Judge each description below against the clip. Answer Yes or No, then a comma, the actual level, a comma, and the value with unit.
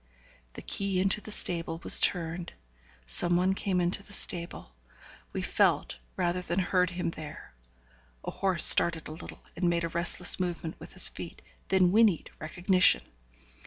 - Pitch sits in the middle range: Yes, medium, 175 Hz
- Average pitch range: No, narrow, 1.8 semitones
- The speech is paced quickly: No, average, 160 wpm